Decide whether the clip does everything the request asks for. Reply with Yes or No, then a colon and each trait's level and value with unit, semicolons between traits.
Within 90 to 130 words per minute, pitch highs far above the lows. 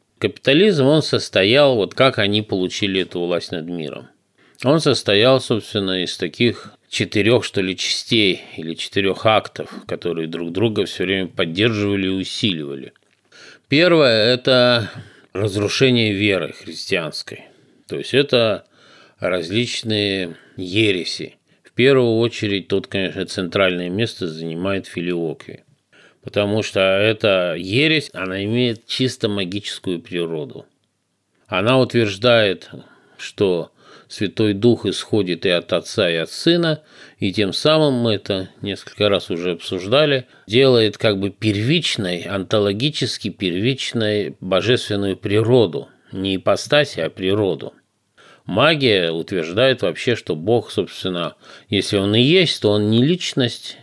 No: average, 120 wpm; average, 4.4 semitones